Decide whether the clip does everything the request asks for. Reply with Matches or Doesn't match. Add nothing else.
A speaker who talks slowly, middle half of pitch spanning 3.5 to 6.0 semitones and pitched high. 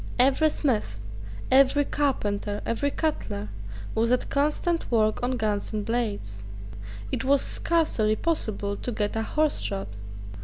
Matches